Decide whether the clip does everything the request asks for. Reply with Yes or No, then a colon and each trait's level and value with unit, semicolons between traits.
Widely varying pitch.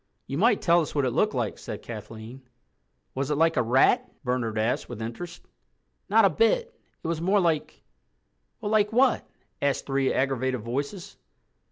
Yes: wide, 7.4 semitones